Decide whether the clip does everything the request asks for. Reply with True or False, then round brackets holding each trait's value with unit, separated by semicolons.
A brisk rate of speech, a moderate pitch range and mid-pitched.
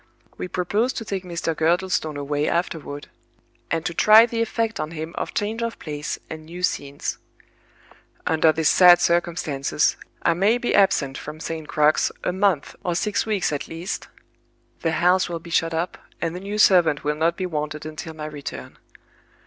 False (175 wpm; 3.3 semitones; 170 Hz)